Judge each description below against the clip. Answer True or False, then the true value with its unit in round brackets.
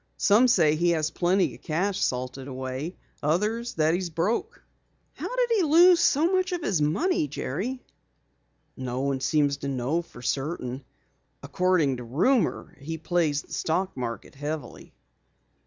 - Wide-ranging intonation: True (7.1 semitones)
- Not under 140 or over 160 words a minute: True (150 wpm)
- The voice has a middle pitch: True (160 Hz)